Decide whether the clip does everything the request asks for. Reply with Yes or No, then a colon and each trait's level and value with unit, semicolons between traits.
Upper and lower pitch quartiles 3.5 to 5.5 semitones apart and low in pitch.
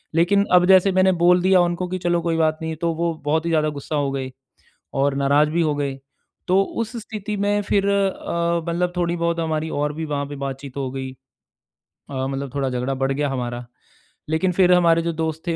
No: average, 3.9 semitones; medium, 165 Hz